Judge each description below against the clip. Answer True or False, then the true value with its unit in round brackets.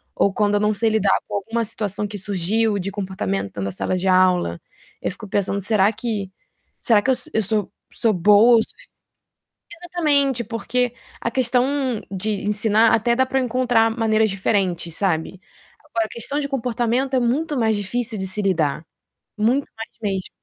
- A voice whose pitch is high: True (215 Hz)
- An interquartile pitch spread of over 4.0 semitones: False (3.4 semitones)